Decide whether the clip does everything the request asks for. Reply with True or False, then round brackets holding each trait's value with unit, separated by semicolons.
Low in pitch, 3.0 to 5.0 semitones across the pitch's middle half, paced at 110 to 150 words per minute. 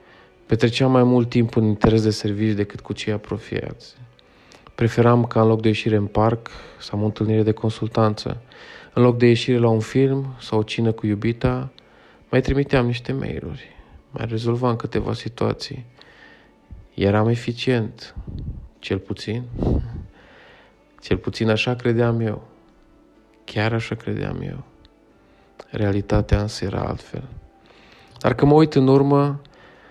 False (115 Hz; 2.4 semitones; 140 wpm)